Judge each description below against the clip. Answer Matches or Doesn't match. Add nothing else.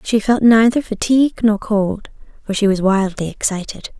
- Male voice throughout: Doesn't match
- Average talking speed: Matches